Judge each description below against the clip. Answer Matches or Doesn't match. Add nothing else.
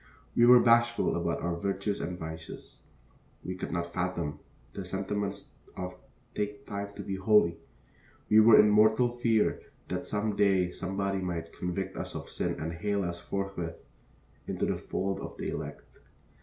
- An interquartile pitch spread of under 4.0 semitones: Matches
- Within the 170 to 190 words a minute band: Doesn't match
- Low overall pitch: Matches